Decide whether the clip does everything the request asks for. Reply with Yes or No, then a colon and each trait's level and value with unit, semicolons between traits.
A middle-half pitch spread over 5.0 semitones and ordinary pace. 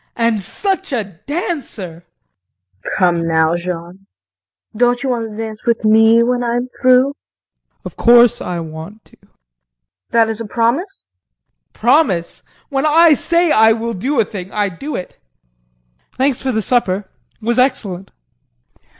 Yes: wide, 5.4 semitones; average, 155 wpm